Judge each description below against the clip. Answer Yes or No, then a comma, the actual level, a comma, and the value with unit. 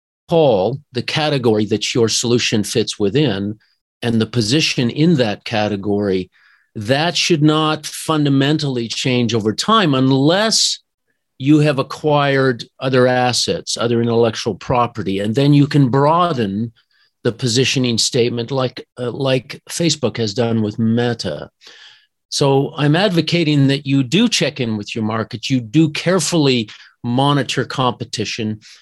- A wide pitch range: No, average, 4.7 semitones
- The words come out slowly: Yes, slow, 130 wpm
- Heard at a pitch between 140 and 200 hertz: No, low, 130 Hz